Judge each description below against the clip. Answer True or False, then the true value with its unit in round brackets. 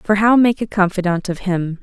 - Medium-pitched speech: False (195 Hz)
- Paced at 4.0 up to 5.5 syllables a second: True (5.0 syllables/s)